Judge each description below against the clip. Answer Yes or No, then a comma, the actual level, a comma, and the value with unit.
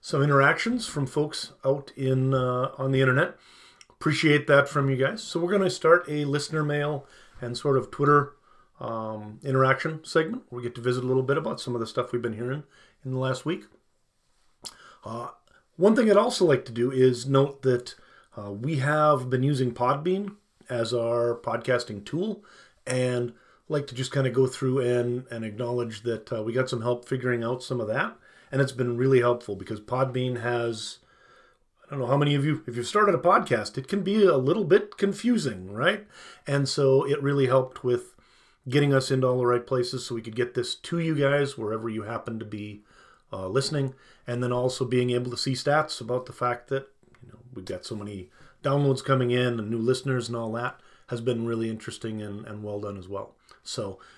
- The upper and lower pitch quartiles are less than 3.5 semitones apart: Yes, average, 2.9 semitones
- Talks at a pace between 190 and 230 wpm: Yes, fast, 205 wpm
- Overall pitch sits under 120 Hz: No, low, 130 Hz